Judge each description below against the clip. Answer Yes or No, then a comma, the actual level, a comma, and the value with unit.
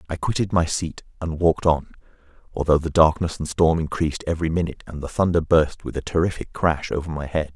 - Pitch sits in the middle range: No, very low, 80 Hz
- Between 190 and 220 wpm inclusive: Yes, fast, 205 wpm